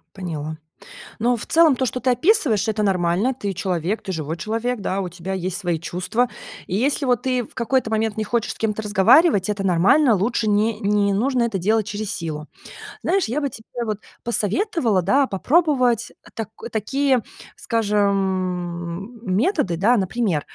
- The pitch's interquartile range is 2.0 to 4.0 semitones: No, average, 4.6 semitones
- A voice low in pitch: No, high, 215 Hz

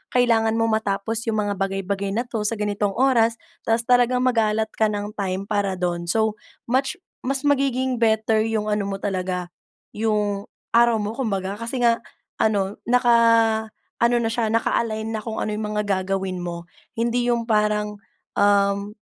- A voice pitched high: Yes, high, 220 Hz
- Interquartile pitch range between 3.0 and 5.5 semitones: No, narrow, 2.5 semitones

